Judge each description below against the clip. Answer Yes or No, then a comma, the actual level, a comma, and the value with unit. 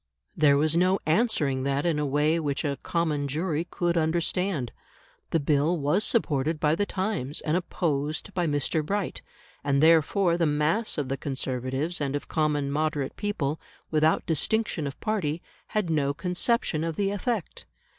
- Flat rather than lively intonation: No, average, 3.5 semitones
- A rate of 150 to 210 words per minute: Yes, average, 160 wpm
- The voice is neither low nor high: Yes, medium, 155 Hz